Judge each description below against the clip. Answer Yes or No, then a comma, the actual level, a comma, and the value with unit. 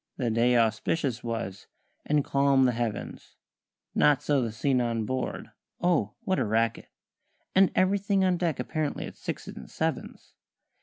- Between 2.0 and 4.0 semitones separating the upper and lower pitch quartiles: No, wide, 5.4 semitones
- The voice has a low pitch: Yes, low, 130 Hz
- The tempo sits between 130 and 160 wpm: Yes, average, 150 wpm